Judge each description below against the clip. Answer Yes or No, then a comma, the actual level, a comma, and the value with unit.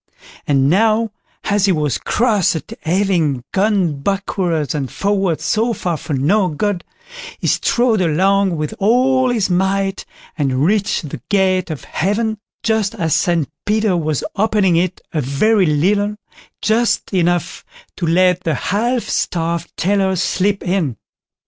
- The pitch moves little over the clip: No, average, 4.2 semitones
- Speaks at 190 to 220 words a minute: No, average, 140 wpm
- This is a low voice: No, high, 190 Hz